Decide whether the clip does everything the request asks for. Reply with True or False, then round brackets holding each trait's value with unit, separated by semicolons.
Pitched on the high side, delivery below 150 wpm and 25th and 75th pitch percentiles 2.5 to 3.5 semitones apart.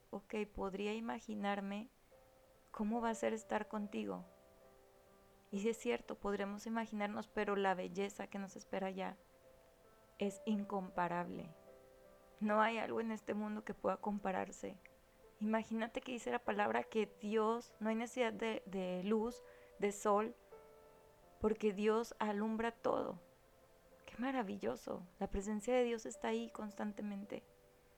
True (210 Hz; 130 wpm; 2.9 semitones)